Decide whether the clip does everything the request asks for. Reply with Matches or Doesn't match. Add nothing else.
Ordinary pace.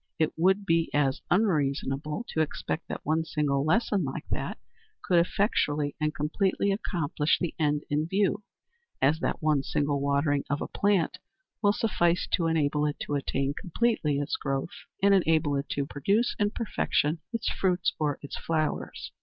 Matches